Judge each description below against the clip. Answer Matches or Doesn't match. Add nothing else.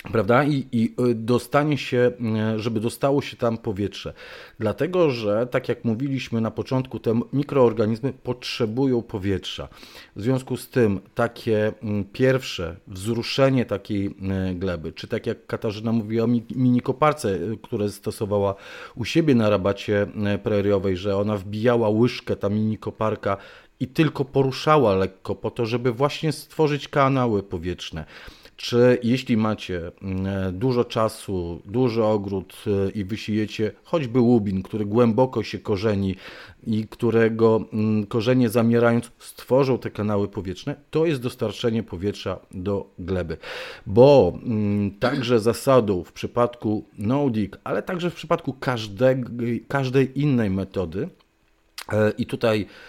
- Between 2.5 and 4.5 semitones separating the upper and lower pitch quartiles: Matches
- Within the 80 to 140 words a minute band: Matches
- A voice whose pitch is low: Matches